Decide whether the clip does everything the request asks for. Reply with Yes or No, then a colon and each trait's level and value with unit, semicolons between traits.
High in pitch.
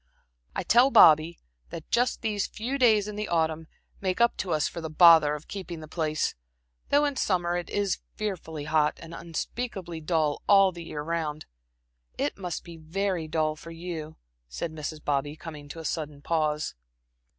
No: medium, 165 Hz